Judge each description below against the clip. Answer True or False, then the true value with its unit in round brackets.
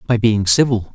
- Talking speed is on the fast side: False (190 wpm)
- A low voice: True (115 Hz)